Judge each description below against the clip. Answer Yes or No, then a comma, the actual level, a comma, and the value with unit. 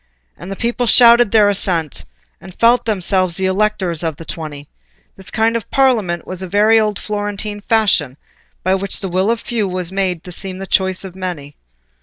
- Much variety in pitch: No, average, 3.0 semitones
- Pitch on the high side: Yes, high, 195 Hz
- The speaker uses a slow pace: No, average, 200 wpm